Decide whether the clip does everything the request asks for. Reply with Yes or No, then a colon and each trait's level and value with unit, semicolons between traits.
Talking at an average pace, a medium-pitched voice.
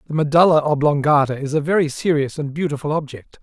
Yes: average, 175 wpm; medium, 150 Hz